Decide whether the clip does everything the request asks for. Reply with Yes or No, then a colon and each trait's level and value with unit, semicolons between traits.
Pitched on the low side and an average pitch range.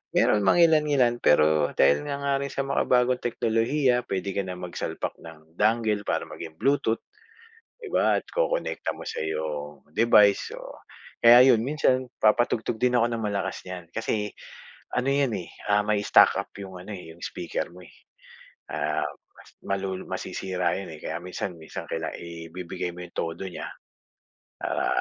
No: low, 100 Hz; wide, 6.0 semitones